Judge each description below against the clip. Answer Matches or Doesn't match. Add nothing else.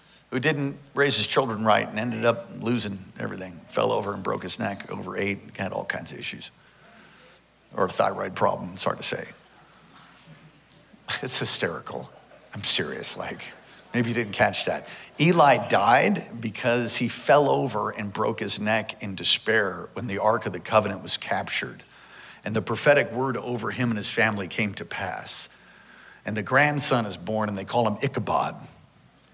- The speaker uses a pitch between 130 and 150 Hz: Doesn't match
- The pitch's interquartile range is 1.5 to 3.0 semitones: Matches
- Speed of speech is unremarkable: Matches